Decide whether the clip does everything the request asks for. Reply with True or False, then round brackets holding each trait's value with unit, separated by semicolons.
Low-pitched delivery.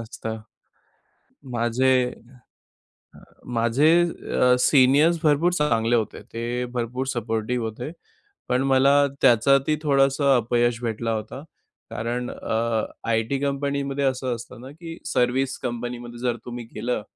True (125 Hz)